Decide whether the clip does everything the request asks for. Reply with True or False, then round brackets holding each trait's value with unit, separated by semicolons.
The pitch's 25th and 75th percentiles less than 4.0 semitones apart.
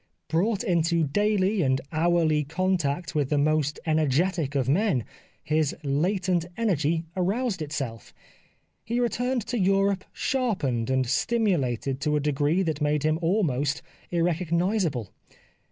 False (4.9 semitones)